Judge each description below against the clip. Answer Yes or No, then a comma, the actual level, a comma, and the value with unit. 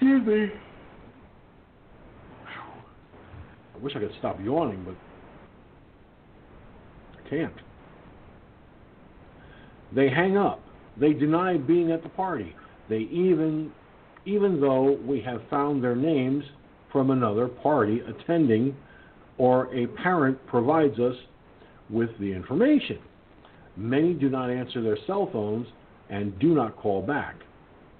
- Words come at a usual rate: No, slow, 115 wpm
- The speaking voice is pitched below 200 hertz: Yes, medium, 140 Hz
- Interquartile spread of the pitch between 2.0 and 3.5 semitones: No, average, 5.2 semitones